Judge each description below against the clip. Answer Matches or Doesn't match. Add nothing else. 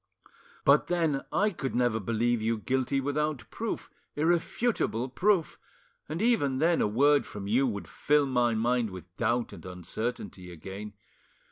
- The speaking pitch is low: Matches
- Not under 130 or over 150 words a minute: Matches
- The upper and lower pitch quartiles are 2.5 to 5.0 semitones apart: Doesn't match